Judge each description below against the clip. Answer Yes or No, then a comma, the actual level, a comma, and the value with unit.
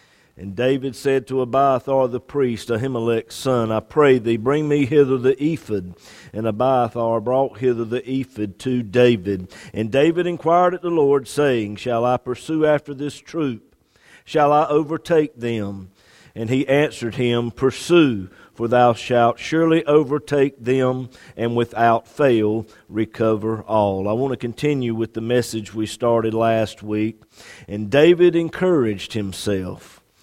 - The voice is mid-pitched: No, low, 125 Hz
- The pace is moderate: Yes, average, 145 wpm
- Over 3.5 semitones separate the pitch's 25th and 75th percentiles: Yes, average, 4.1 semitones